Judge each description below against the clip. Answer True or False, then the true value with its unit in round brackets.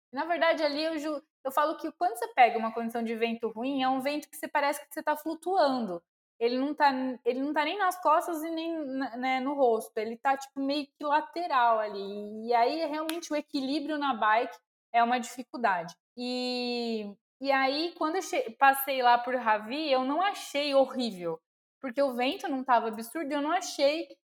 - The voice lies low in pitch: False (275 Hz)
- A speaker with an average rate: False (200 wpm)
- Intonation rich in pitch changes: False (4.3 semitones)